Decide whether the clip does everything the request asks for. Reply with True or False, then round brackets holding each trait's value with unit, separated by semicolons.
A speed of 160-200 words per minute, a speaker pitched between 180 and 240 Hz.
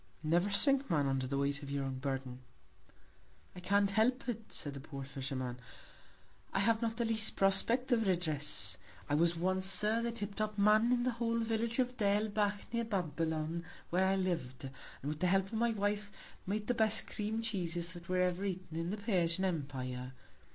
True (185 wpm; 190 Hz)